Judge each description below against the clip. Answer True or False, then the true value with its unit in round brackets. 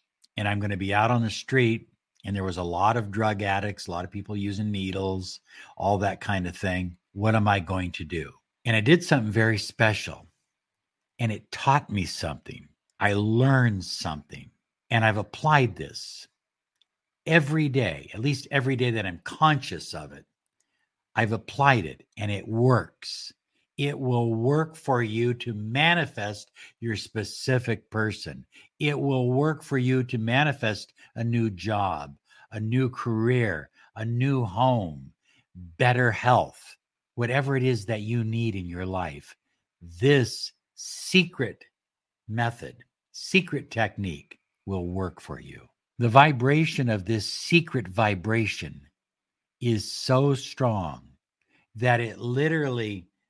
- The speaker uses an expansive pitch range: False (4.8 semitones)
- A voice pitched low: True (110 Hz)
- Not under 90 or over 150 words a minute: True (145 wpm)